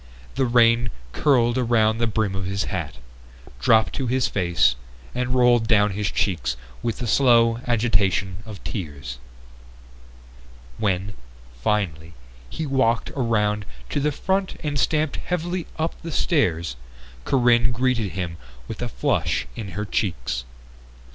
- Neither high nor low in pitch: No, low, 115 Hz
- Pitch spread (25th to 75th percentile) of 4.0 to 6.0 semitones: Yes, average, 4.7 semitones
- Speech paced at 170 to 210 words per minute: No, slow, 135 wpm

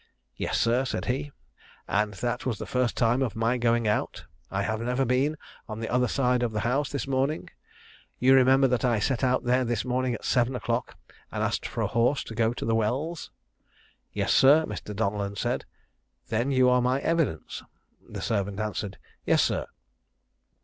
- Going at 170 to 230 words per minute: Yes, average, 185 wpm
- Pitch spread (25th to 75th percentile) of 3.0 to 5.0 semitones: No, narrow, 2.6 semitones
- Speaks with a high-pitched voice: No, low, 125 Hz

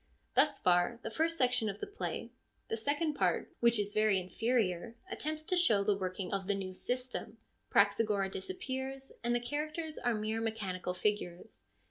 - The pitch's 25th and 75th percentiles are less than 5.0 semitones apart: No, average, 5.3 semitones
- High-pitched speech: Yes, high, 225 Hz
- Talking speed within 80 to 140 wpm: No, average, 165 wpm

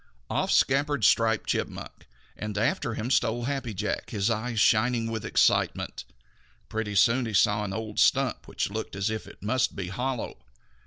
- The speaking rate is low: No, average, 165 wpm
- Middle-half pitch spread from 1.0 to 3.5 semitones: Yes, narrow, 2.6 semitones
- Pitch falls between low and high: No, low, 110 Hz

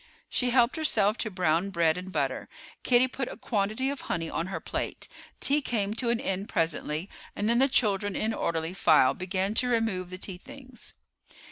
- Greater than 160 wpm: Yes, average, 190 wpm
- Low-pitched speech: No, high, 205 Hz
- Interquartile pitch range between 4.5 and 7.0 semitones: Yes, average, 4.9 semitones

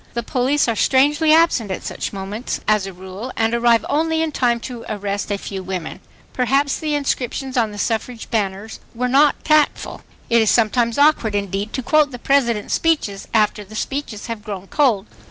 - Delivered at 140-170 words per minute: No, average, 185 wpm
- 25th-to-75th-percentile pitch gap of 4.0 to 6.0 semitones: Yes, average, 5.0 semitones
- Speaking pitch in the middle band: No, high, 235 Hz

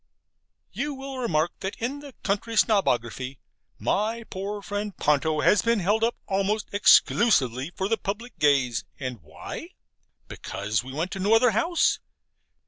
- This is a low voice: No, high, 200 Hz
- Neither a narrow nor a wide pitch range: No, wide, 7.6 semitones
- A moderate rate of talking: Yes, average, 145 wpm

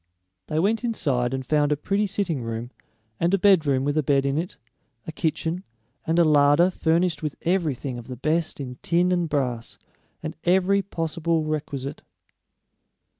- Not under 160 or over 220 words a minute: Yes, average, 165 wpm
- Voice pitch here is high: No, medium, 155 Hz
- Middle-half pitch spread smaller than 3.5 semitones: No, average, 4.0 semitones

